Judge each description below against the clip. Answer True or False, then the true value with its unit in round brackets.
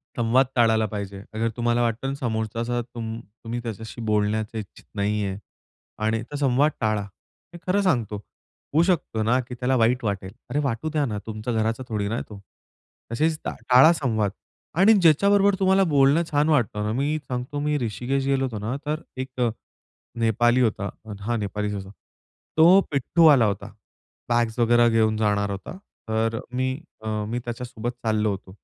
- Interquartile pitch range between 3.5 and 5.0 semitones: True (4.0 semitones)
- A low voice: True (120 Hz)